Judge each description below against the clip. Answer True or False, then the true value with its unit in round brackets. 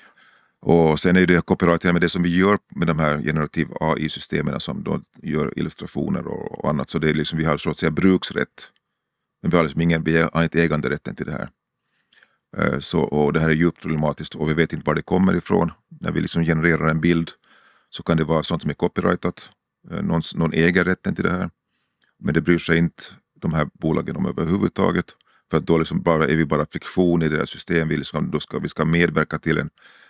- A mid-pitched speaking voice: False (80 Hz)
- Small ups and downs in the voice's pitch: True (1.6 semitones)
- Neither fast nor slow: False (215 wpm)